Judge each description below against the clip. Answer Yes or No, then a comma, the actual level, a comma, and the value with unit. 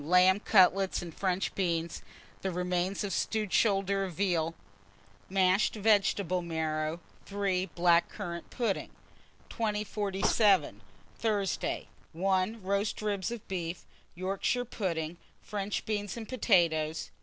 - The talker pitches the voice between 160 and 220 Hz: Yes, high, 190 Hz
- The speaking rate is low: Yes, slow, 110 wpm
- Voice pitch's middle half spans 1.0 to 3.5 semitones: Yes, average, 2.8 semitones